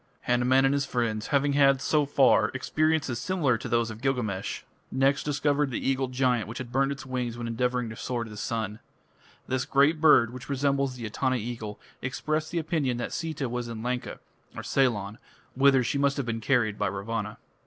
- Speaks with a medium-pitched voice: No, low, 130 Hz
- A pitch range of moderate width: Yes, average, 3.1 semitones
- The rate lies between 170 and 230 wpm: Yes, average, 190 wpm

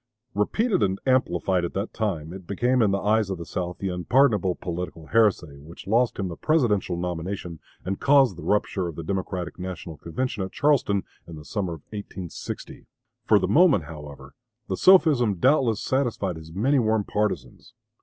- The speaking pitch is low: Yes, very low, 95 Hz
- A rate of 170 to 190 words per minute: Yes, average, 175 wpm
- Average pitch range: Yes, average, 4.8 semitones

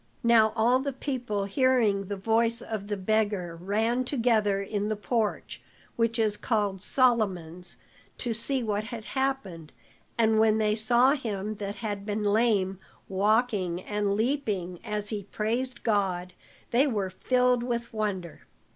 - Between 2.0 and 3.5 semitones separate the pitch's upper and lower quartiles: Yes, average, 2.9 semitones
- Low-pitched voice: No, high, 215 Hz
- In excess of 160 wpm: No, average, 145 wpm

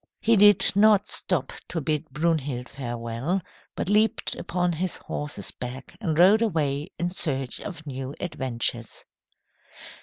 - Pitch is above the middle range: No, medium, 155 Hz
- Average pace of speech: No, slow, 130 wpm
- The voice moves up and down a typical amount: No, wide, 5.7 semitones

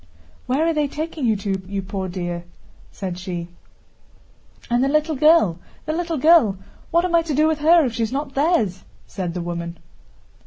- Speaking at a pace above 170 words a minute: Yes, average, 185 wpm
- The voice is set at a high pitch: Yes, very high, 255 Hz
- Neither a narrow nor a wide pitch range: No, wide, 8.9 semitones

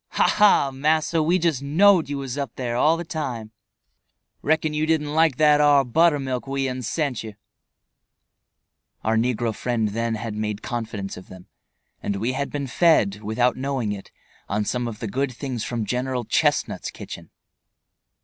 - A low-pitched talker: Yes, low, 130 Hz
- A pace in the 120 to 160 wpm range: No, average, 170 wpm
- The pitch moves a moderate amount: Yes, average, 4.9 semitones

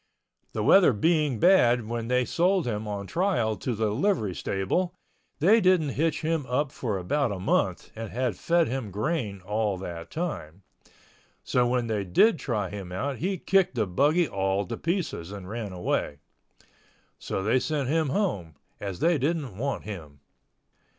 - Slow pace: No, average, 165 wpm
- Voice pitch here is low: Yes, low, 120 Hz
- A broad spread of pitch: Yes, wide, 8.2 semitones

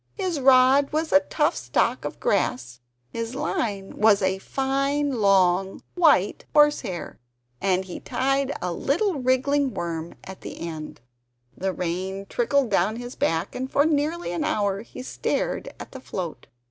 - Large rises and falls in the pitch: Yes, wide, 6.9 semitones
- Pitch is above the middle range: Yes, high, 230 Hz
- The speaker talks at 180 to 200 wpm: No, average, 155 wpm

